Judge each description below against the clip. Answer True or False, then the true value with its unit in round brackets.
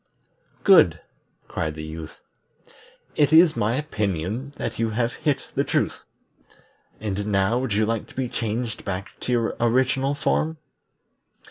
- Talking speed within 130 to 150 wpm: True (140 wpm)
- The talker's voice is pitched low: True (115 Hz)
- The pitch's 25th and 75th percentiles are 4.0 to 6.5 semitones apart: True (4.5 semitones)